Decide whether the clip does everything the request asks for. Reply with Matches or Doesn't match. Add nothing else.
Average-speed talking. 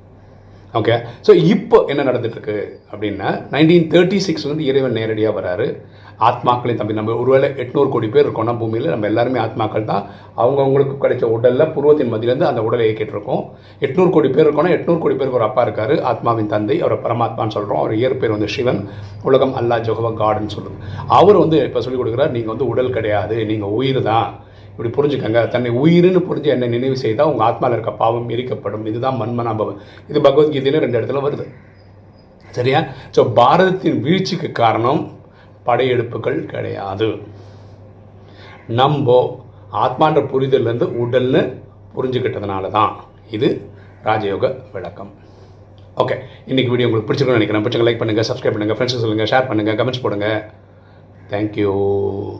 Doesn't match